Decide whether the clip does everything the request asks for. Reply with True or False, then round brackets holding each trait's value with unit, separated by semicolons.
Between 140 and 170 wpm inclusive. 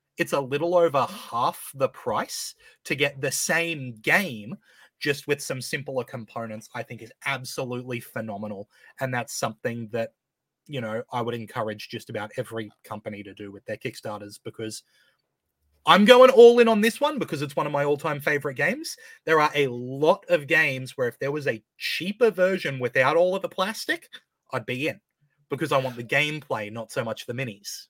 False (185 wpm)